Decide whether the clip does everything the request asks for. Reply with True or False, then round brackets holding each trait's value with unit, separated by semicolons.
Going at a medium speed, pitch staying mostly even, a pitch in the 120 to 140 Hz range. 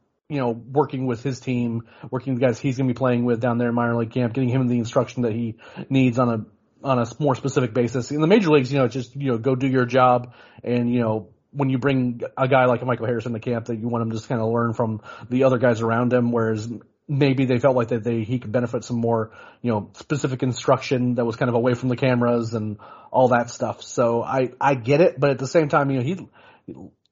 False (265 wpm; 2.1 semitones; 125 Hz)